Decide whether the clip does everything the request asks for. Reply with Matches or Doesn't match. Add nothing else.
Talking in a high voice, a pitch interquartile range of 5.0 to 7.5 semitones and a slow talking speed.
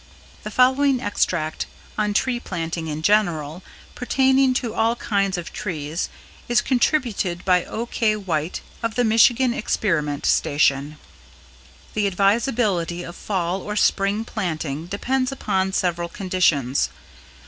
Matches